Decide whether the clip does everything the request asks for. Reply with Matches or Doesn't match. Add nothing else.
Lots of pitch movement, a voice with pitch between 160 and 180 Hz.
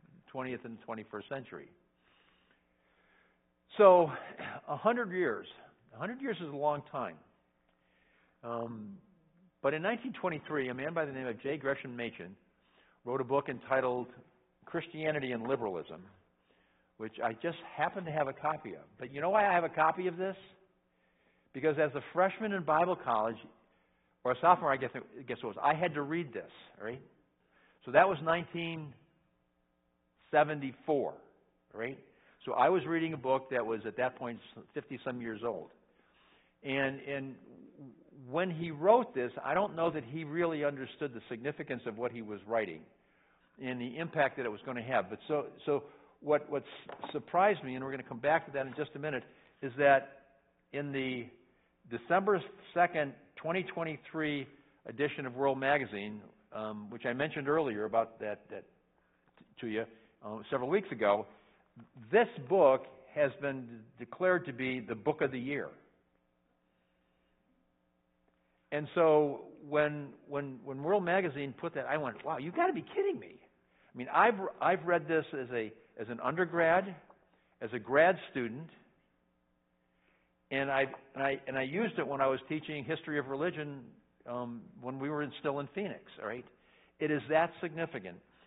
Doesn't match